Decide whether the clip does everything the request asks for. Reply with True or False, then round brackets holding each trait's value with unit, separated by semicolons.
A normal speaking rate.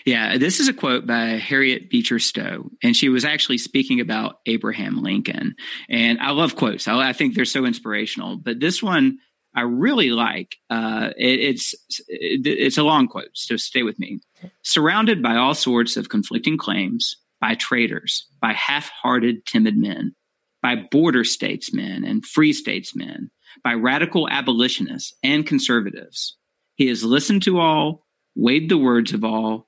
True (160 wpm)